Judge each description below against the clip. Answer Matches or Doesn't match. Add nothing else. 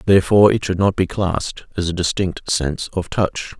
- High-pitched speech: Doesn't match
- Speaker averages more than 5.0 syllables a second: Matches